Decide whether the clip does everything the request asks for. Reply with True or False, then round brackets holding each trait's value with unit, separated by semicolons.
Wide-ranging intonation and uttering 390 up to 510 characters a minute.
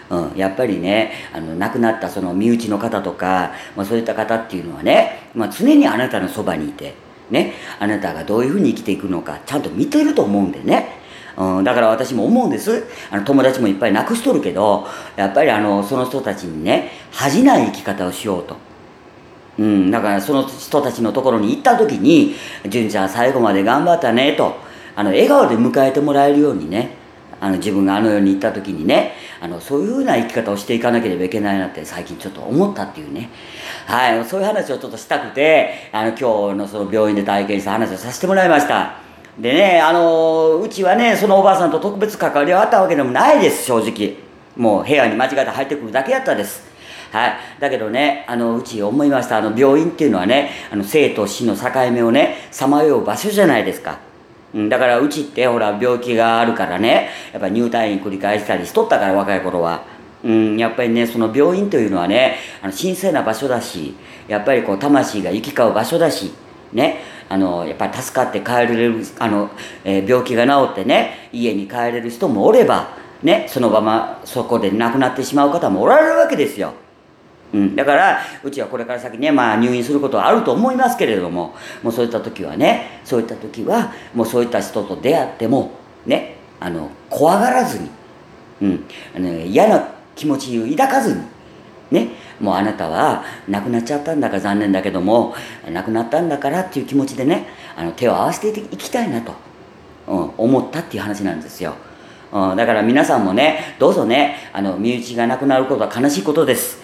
True (5.7 semitones; 410 characters per minute)